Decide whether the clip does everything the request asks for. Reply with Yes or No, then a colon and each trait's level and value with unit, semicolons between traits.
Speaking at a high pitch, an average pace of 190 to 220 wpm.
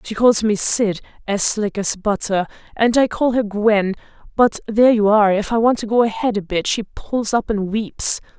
Yes: high, 215 Hz; fast, 205 wpm